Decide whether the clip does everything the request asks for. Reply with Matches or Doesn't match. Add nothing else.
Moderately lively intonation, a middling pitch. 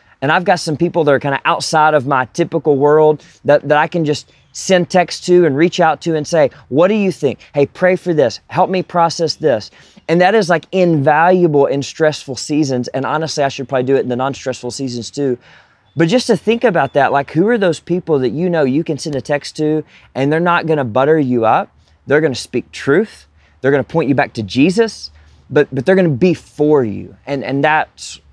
Matches